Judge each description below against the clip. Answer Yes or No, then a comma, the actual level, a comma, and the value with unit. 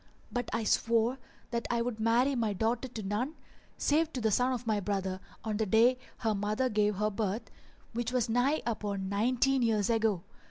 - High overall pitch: Yes, high, 225 Hz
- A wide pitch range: No, average, 2.8 semitones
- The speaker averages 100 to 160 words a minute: No, average, 190 wpm